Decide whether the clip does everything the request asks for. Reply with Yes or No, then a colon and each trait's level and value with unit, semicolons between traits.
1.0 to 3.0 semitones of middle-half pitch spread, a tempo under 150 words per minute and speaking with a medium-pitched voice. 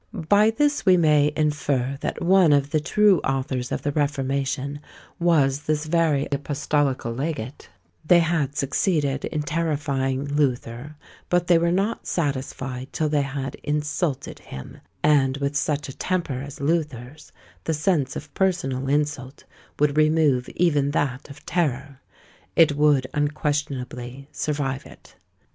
Yes: narrow, 2.6 semitones; slow, 135 wpm; medium, 145 Hz